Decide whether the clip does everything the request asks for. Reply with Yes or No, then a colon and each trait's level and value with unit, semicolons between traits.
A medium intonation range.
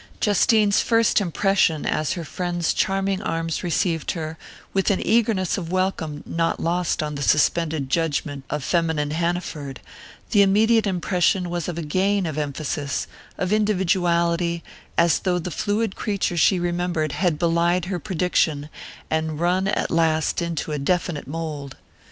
Yes: average, 3.1 semitones